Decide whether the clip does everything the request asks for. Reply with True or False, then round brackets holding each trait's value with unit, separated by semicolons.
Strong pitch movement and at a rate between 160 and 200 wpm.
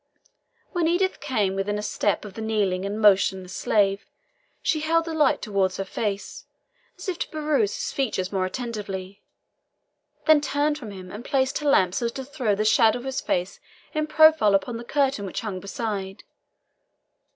True (6.6 semitones; 180 wpm)